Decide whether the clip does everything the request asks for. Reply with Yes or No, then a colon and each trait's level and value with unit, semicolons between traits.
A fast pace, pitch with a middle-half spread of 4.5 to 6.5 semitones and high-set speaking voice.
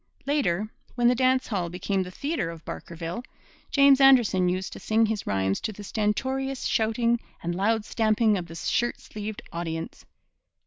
No: average, 165 wpm; average, 5.3 semitones; high, 215 Hz